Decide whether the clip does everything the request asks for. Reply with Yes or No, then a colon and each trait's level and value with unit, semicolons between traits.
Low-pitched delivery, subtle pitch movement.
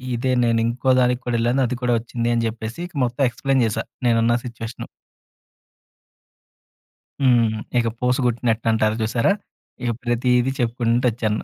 Yes: low, 120 Hz; narrow, 1.4 semitones